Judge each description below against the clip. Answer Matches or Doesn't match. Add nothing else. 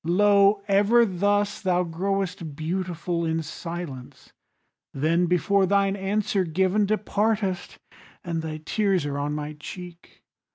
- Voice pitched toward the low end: Doesn't match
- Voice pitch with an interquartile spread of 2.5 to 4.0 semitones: Matches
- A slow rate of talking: Matches